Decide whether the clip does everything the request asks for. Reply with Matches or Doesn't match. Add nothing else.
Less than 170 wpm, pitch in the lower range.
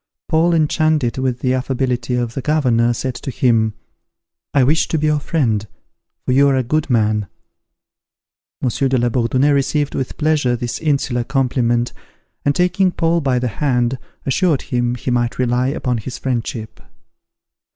Matches